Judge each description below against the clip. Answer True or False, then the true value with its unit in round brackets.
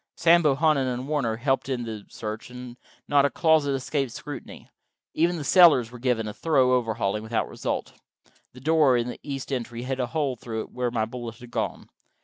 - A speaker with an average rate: True (195 wpm)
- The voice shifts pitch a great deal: False (3.3 semitones)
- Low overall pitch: True (125 Hz)